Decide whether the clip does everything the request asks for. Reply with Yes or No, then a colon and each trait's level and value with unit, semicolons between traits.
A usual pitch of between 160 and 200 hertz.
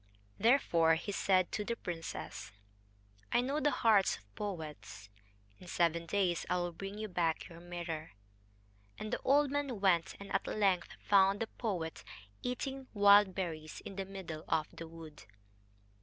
Yes: high, 190 Hz